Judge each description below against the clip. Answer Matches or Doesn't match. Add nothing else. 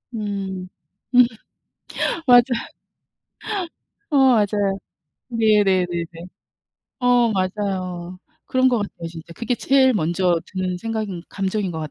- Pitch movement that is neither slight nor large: Matches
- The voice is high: Matches